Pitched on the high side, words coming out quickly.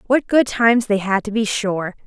Yes: high, 215 Hz; fast, 235 wpm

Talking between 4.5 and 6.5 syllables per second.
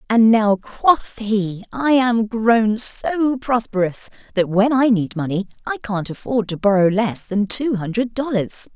No: 4.0 syllables/s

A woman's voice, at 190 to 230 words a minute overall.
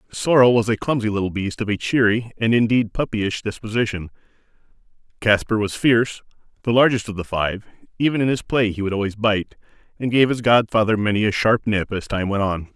No: male; average, 195 wpm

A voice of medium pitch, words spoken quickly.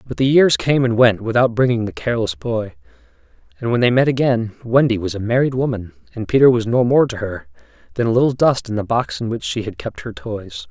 No: low, 115 Hz; fast, 235 wpm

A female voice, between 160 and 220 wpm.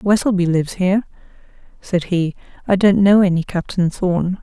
No: female; average, 150 wpm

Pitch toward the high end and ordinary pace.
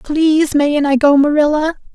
Yes: very high, 295 Hz; average, 155 wpm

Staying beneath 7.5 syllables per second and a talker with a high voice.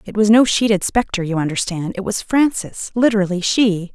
Yes: 5.3 syllables/s; high, 205 Hz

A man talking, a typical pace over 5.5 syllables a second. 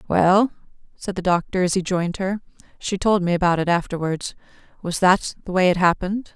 No: female; 5.7 syllables/s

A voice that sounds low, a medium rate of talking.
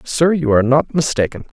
No: medium, 145 Hz; average, 190 wpm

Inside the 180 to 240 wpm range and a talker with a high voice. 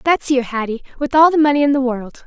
No: fast, 265 wpm; very high, 270 Hz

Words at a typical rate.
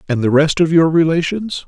No: fast, 215 wpm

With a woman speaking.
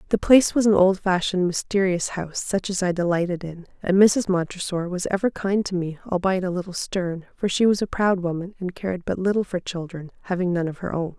Yes: female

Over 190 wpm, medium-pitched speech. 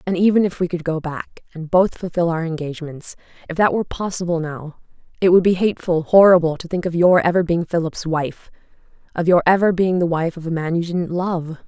Yes: average, 200 wpm; medium, 170 Hz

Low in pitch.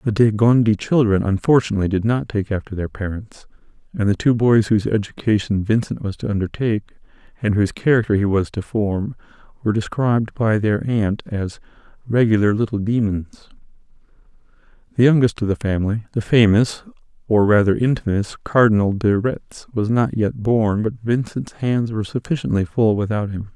Yes: low, 110 Hz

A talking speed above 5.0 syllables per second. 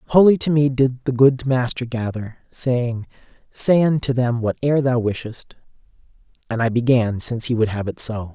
No: 4.9 syllables/s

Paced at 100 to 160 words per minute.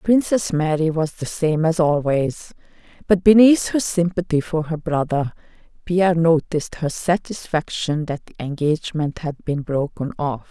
Yes: average, 145 wpm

